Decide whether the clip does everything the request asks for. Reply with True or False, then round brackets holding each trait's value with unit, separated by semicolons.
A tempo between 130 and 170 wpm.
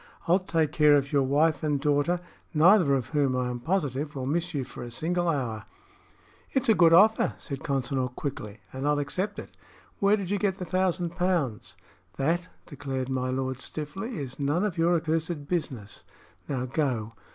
False (180 wpm)